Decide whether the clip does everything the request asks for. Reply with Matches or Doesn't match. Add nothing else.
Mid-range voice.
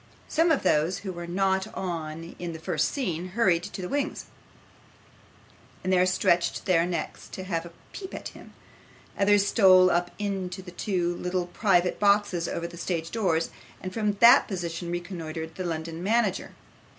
Matches